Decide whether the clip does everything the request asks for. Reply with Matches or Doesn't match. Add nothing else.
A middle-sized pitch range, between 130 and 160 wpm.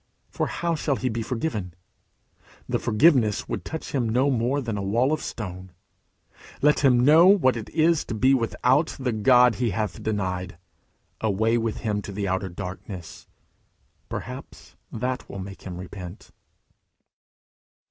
Matches